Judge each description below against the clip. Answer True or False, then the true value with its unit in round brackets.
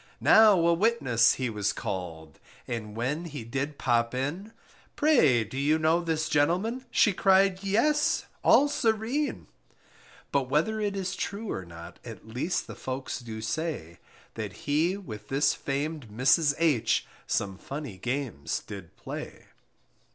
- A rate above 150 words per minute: False (145 wpm)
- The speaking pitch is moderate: True (145 Hz)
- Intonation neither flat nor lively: False (8.5 semitones)